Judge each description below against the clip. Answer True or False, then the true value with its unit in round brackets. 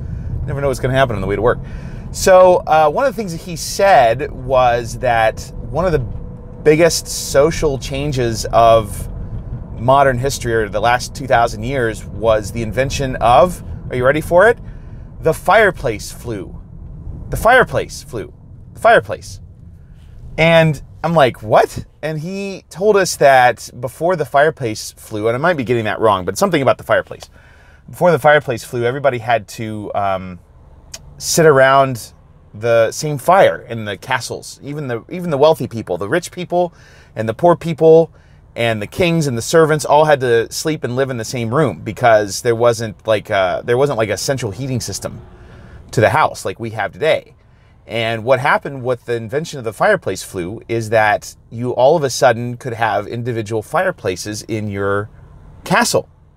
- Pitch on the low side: True (120 Hz)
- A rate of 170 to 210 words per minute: True (175 wpm)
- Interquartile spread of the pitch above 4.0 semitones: True (4.7 semitones)